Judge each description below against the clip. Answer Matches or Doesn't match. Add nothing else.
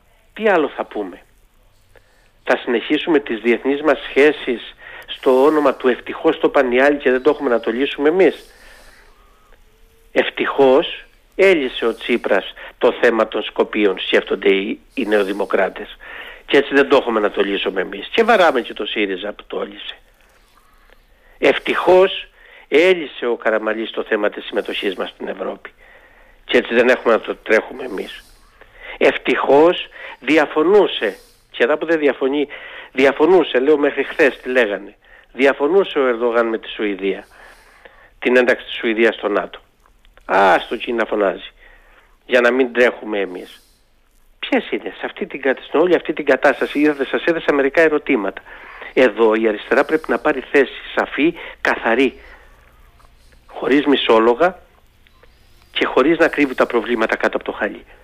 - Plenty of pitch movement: Matches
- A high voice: Doesn't match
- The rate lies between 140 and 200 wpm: Matches